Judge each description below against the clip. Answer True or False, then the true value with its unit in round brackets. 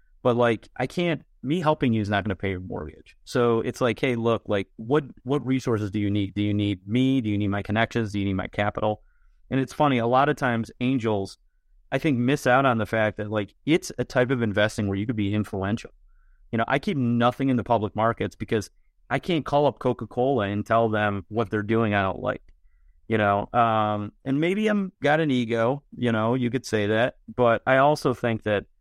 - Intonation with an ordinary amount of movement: True (3.7 semitones)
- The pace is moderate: False (230 wpm)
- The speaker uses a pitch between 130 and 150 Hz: False (115 Hz)